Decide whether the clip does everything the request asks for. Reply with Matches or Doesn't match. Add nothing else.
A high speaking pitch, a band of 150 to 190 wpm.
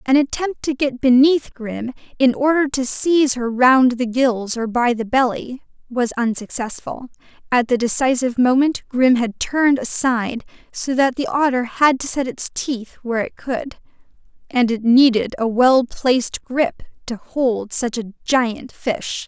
Matches